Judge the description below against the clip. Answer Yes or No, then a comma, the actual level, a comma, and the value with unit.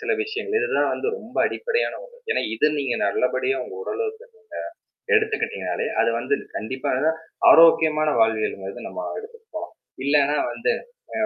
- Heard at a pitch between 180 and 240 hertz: No, very high, 320 Hz